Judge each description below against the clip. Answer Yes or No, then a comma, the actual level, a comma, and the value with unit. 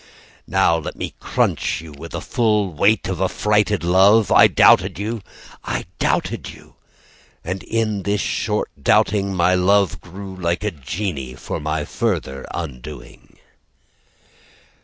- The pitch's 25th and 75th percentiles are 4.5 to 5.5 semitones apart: No, average, 4.0 semitones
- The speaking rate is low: Yes, slow, 130 wpm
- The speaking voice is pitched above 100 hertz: No, very low, 95 Hz